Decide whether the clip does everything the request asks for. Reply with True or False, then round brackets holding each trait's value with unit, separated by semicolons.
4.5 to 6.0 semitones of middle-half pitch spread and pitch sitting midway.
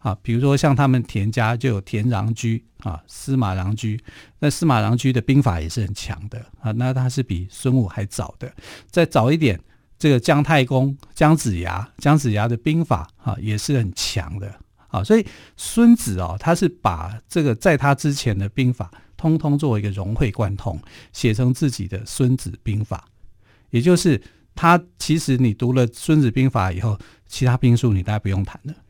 False (5.1 semitones; 120 Hz)